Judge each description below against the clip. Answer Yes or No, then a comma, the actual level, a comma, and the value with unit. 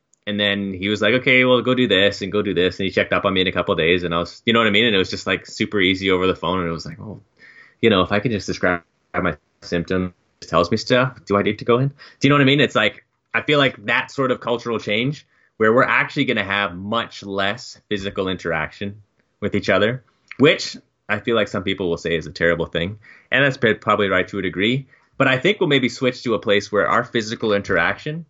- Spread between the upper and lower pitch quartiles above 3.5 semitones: Yes, average, 4.9 semitones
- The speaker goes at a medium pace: No, fast, 275 wpm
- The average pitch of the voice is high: No, low, 105 Hz